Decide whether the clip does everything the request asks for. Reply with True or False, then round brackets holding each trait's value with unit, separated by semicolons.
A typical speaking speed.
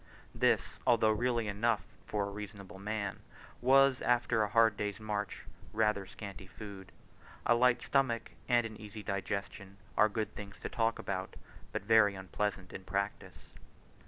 True (145 wpm)